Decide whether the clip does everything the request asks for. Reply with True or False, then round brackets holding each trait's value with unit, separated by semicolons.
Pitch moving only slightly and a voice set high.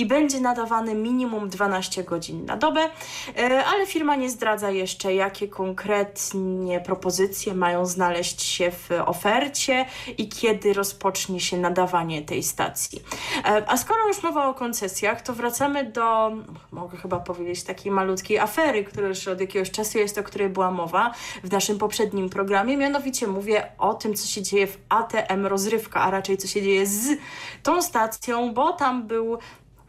False (4.0 semitones; 205 Hz)